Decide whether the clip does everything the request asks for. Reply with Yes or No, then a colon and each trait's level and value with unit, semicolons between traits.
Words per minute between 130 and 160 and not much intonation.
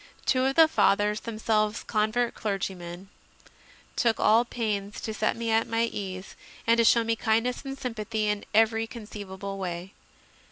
Yes: average, 155 wpm; narrow, 2.2 semitones